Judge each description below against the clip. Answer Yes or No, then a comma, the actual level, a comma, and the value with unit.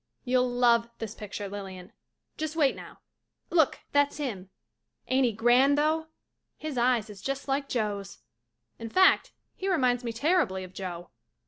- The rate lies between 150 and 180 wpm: Yes, average, 155 wpm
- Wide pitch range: Yes, wide, 5.7 semitones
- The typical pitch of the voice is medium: No, high, 245 Hz